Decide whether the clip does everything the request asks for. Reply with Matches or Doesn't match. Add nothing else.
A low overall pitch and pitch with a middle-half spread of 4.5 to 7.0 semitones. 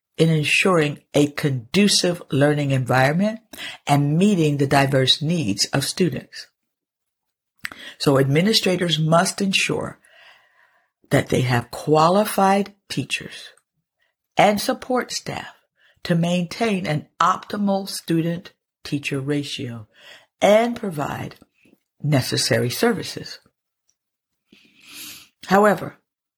Doesn't match